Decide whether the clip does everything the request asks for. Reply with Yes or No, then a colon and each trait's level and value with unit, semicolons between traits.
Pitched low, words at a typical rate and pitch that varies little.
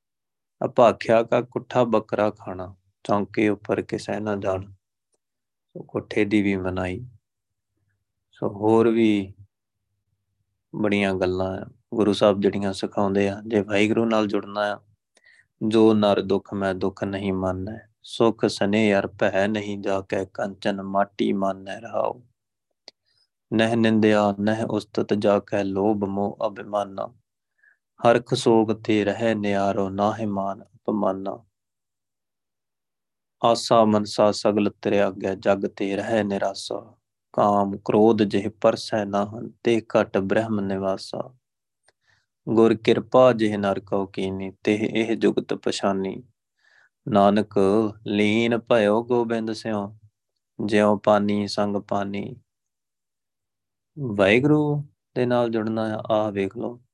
Yes: low, 105 Hz; average, 115 wpm; narrow, 1.9 semitones